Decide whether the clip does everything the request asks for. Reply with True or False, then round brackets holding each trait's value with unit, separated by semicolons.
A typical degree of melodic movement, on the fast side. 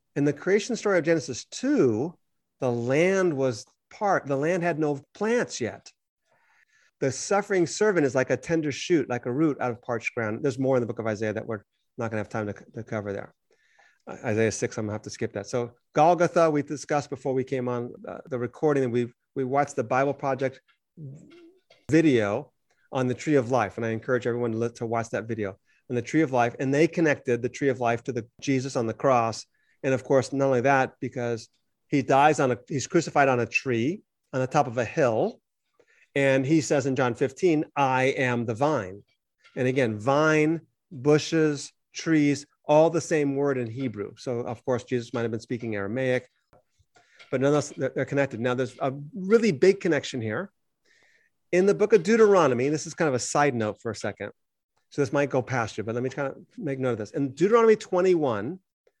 True (4.2 semitones; 210 wpm)